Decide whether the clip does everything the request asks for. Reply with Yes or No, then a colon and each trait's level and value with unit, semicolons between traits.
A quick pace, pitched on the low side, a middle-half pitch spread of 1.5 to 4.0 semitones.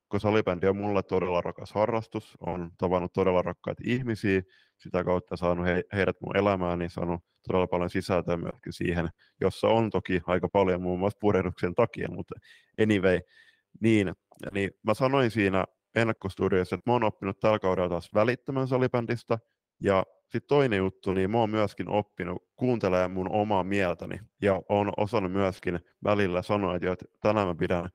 Yes: fast, 160 wpm; very low, 95 Hz; average, 2.9 semitones